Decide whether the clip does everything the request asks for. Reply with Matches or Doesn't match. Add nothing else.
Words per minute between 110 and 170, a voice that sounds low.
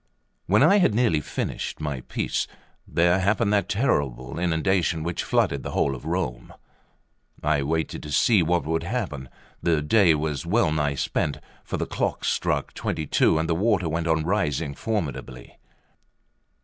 Matches